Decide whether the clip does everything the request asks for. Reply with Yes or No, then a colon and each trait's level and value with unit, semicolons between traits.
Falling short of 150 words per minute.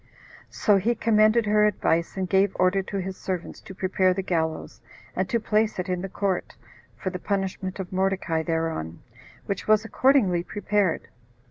No: average, 165 wpm